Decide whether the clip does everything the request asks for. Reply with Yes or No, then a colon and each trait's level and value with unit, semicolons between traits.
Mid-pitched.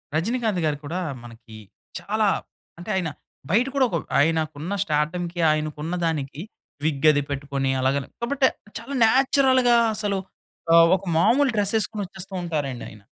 Yes: medium, 170 Hz